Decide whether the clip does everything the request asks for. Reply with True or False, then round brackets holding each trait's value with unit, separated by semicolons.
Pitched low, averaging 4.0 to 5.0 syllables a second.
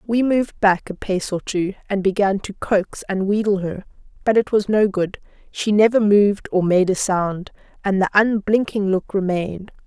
False (200 Hz; 4.7 syllables/s)